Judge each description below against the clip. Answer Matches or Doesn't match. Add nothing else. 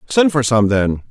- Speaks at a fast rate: Matches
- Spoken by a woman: Doesn't match